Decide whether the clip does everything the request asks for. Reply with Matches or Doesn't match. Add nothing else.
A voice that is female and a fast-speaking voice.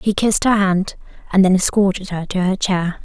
Matches